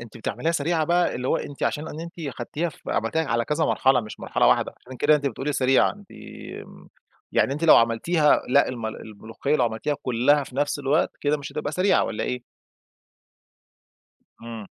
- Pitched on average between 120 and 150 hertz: Yes, medium, 140 Hz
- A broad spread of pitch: No, average, 4.4 semitones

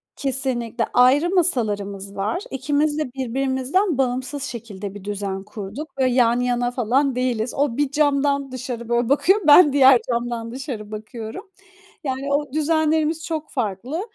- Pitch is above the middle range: Yes, very high, 260 Hz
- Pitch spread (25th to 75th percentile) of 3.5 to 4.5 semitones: Yes, average, 3.9 semitones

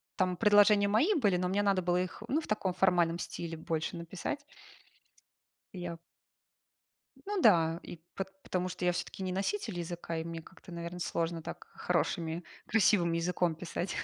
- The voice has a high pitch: No, medium, 180 Hz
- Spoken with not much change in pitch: No, average, 3.0 semitones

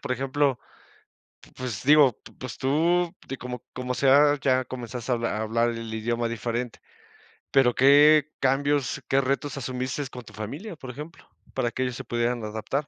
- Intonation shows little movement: No, average, 3.0 semitones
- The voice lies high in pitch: No, low, 130 Hz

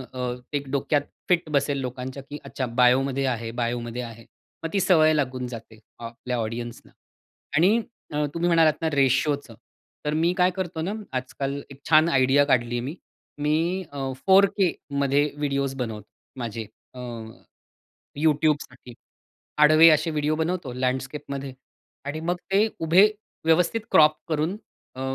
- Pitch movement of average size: Yes, average, 3.9 semitones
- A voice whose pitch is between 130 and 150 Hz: Yes, medium, 140 Hz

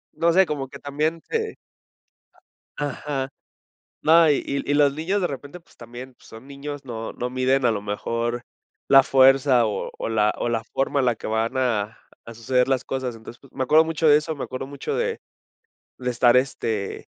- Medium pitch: No, low, 130 Hz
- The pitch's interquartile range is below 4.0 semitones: Yes, average, 3.5 semitones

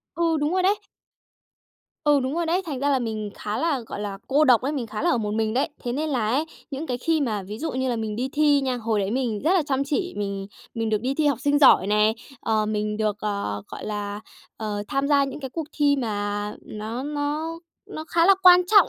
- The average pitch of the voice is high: Yes, very high, 255 Hz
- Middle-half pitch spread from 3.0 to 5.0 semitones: No, wide, 5.6 semitones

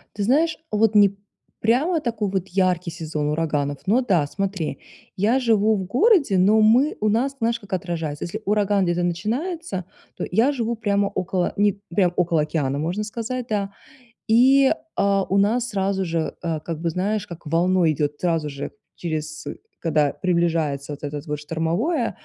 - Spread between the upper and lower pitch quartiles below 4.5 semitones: No, average, 5.0 semitones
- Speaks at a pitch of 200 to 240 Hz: No, high, 190 Hz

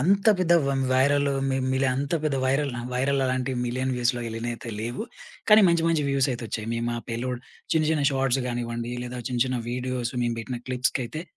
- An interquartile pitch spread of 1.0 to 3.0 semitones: Yes, narrow, 2.5 semitones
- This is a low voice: Yes, low, 130 Hz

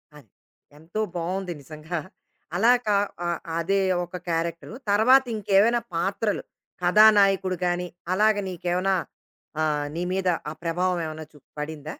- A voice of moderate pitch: Yes, medium, 180 Hz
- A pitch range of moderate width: Yes, average, 3.4 semitones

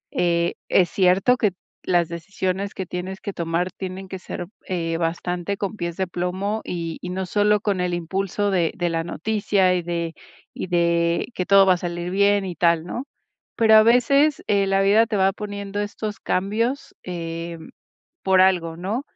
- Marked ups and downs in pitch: No, average, 2.7 semitones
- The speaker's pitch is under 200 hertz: Yes, medium, 185 Hz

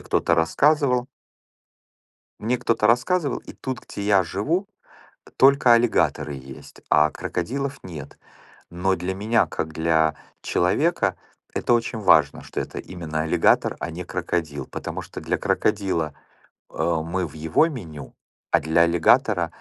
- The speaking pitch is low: Yes, very low, 90 Hz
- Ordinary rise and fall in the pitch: No, wide, 6.7 semitones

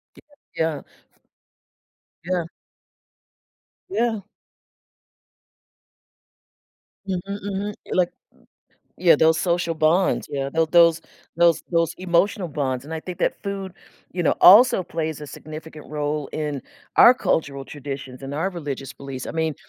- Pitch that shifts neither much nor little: Yes, average, 3.6 semitones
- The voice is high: No, medium, 160 Hz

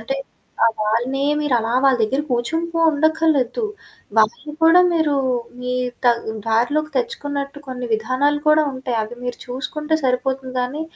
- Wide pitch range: No, average, 3.6 semitones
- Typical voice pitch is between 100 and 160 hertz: No, very high, 270 Hz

